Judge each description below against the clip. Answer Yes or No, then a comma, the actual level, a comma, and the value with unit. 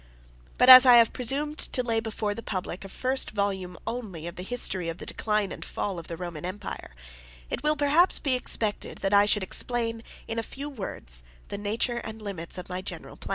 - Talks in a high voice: Yes, high, 210 Hz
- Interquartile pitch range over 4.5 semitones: Yes, average, 4.9 semitones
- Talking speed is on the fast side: Yes, fast, 215 wpm